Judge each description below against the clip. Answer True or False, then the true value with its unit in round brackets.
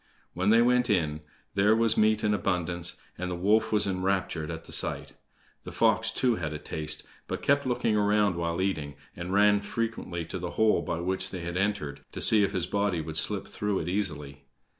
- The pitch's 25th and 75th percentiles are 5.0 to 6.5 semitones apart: False (3.7 semitones)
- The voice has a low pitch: True (95 Hz)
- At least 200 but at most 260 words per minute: True (205 wpm)